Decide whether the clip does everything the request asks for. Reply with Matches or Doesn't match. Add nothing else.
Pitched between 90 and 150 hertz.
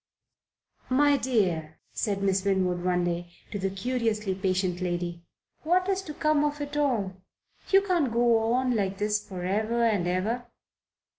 Doesn't match